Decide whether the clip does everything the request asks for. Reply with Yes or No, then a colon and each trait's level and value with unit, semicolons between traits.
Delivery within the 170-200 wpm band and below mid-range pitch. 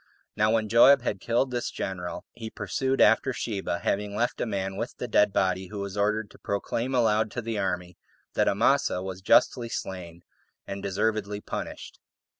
Yes: average, 175 wpm; low, 105 Hz